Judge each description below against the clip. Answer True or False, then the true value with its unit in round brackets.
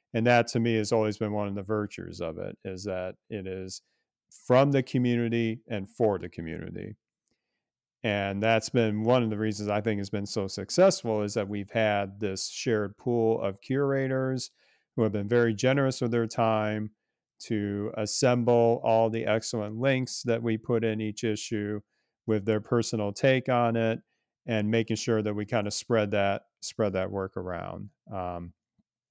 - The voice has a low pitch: True (110 Hz)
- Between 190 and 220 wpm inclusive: False (175 wpm)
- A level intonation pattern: True (2.3 semitones)